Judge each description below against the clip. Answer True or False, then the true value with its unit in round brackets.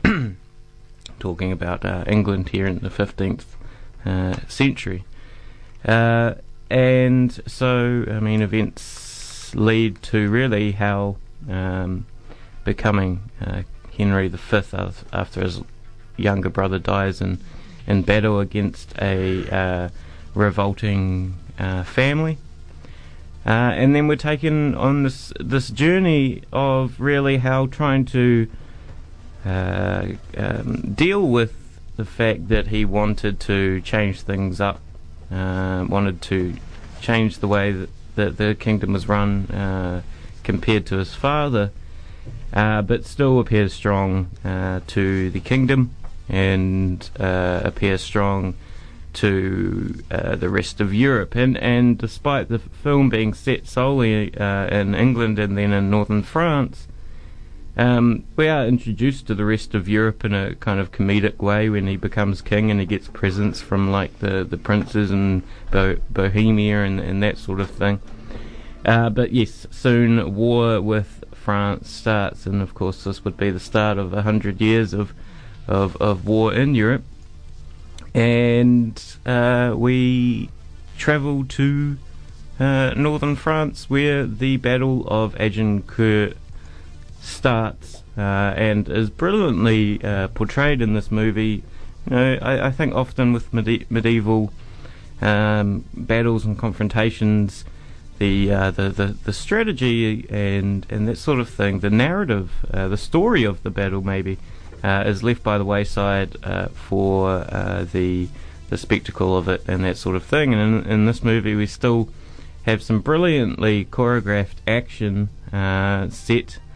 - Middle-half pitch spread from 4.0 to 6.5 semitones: False (3.4 semitones)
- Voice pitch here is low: True (105 Hz)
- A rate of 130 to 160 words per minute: True (140 wpm)